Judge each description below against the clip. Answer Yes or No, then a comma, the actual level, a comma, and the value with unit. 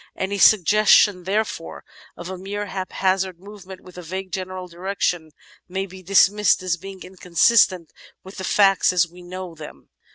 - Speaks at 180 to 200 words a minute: No, average, 155 wpm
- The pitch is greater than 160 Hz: Yes, medium, 185 Hz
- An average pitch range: No, narrow, 1.6 semitones